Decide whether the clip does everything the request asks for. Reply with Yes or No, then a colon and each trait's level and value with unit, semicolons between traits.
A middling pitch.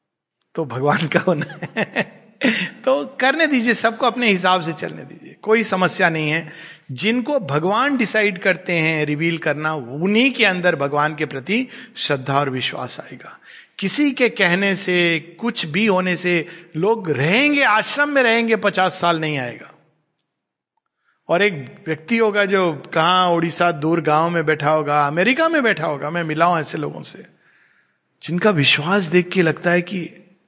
Yes: medium, 175 Hz